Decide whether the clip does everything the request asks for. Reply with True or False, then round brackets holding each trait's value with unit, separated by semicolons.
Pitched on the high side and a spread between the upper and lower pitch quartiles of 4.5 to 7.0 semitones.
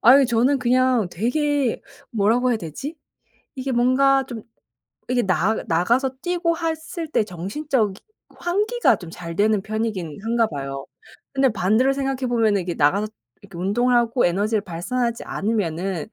True (230 Hz; 5.5 semitones)